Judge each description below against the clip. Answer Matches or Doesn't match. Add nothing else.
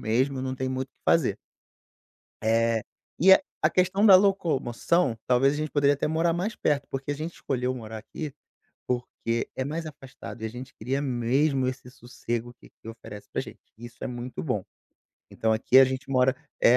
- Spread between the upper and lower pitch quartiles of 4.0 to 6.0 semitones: Doesn't match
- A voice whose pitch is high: Doesn't match